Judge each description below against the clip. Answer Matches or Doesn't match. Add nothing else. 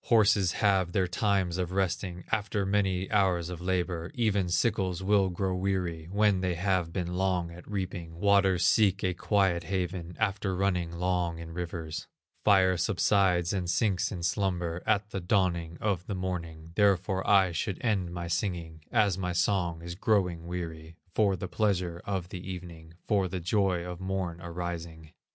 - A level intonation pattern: Matches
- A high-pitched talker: Doesn't match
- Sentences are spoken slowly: Doesn't match